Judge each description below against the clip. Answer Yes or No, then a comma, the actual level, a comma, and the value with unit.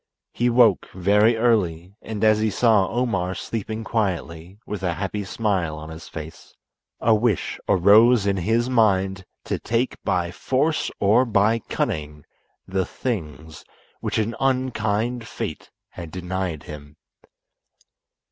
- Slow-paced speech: Yes, slow, 130 wpm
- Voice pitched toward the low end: Yes, low, 100 Hz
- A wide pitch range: No, average, 4.5 semitones